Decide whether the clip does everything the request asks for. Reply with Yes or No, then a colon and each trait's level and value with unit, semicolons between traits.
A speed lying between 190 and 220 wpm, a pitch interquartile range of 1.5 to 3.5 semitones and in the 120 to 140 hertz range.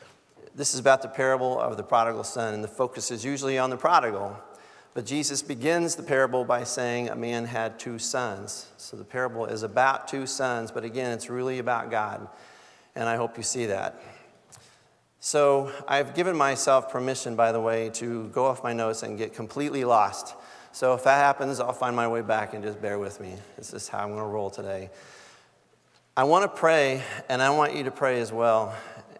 Yes: fast, 205 wpm; average, 3.0 semitones; low, 125 Hz